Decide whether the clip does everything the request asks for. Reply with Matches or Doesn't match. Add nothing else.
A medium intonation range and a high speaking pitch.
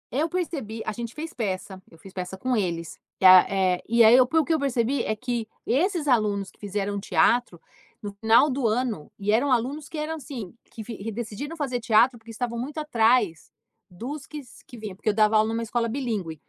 Matches